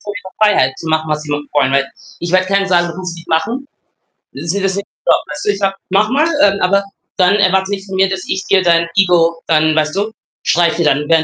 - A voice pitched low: No, medium, 180 Hz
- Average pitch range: Yes, average, 3.6 semitones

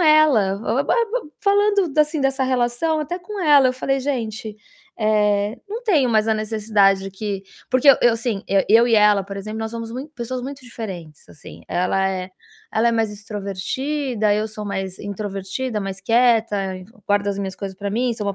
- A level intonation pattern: No, average, 4.5 semitones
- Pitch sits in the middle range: No, high, 220 Hz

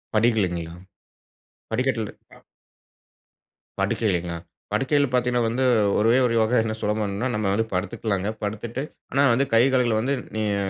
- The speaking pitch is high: No, low, 110 Hz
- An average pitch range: Yes, average, 3.0 semitones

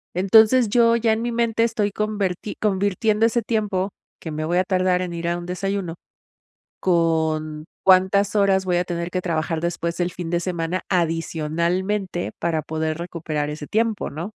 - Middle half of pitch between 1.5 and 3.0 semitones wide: No, average, 3.5 semitones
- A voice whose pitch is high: No, medium, 180 Hz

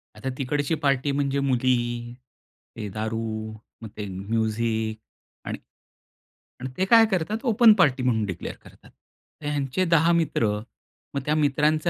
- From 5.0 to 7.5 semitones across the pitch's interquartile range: Yes, average, 5.3 semitones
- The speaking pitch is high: No, low, 130 Hz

